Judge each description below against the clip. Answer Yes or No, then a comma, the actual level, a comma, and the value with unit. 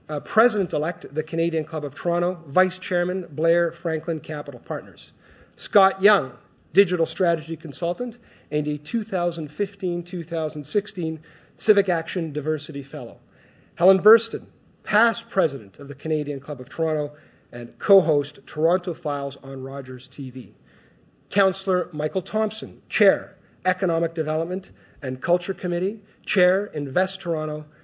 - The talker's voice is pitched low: No, medium, 165 Hz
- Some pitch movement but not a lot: Yes, average, 3.7 semitones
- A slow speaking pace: Yes, slow, 125 wpm